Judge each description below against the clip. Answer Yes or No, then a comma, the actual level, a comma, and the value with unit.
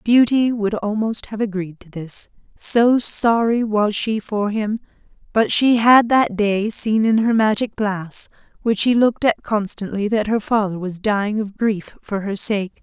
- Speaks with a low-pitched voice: No, high, 215 Hz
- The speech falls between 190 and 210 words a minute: No, average, 180 wpm